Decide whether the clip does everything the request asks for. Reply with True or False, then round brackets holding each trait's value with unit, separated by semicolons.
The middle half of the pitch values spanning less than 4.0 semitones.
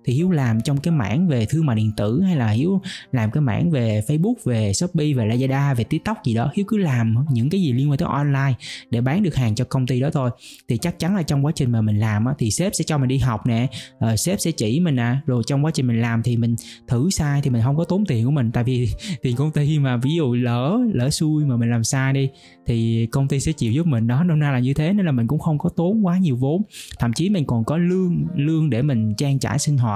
False (5.1 semitones)